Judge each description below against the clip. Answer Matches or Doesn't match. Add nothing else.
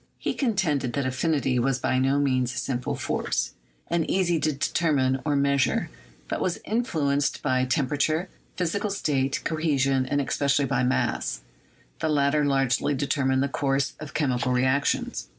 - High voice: Doesn't match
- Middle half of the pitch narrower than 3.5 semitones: Matches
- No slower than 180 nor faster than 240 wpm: Doesn't match